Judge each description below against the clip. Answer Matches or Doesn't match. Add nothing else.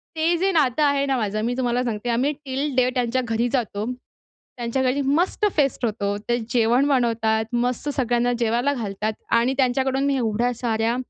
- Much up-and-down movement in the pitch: Doesn't match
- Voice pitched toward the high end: Matches